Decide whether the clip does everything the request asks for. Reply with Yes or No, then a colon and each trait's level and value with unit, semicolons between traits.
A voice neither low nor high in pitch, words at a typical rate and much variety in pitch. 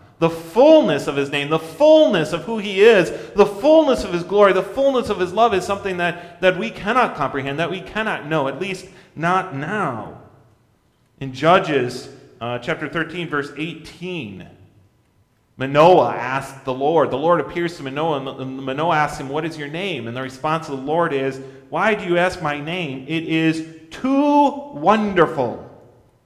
Yes: medium, 165 Hz; average, 175 wpm; wide, 5.8 semitones